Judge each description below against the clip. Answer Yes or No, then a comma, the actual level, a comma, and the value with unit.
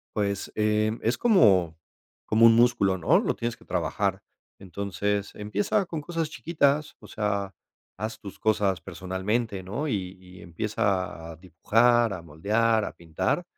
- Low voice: Yes, low, 105 Hz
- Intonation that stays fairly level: No, average, 3.8 semitones